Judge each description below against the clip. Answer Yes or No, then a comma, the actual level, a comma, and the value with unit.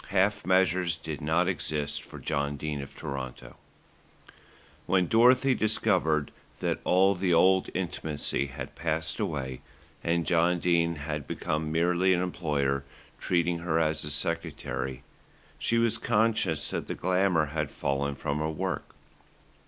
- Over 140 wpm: No, slow, 135 wpm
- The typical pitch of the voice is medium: No, very low, 80 Hz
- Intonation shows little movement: No, average, 3.7 semitones